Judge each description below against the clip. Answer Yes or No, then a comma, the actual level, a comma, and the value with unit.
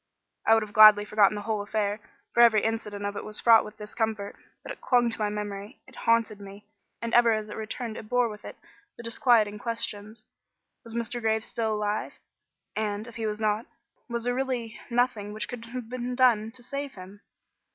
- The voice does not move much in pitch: Yes, narrow, 2.1 semitones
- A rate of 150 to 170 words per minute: No, fast, 205 wpm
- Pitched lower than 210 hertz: No, high, 220 Hz